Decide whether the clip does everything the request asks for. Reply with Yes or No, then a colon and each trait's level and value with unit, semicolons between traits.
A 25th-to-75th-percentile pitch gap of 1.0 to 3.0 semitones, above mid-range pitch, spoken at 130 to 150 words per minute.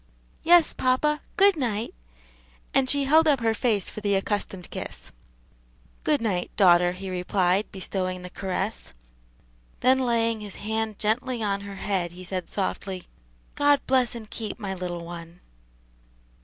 No: average, 5.3 semitones; high, 210 Hz; average, 145 wpm